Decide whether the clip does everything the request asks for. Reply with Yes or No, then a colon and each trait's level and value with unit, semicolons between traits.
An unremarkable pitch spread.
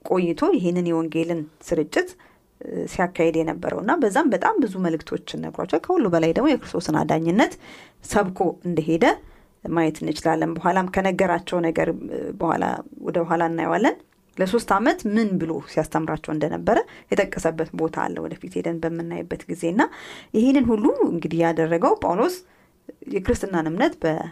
Yes: average, 3.2 semitones